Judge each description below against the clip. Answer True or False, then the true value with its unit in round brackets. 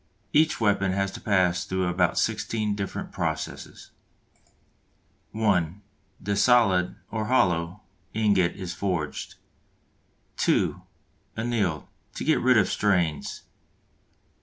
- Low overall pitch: True (100 Hz)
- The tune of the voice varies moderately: True (3.4 semitones)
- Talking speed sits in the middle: False (105 wpm)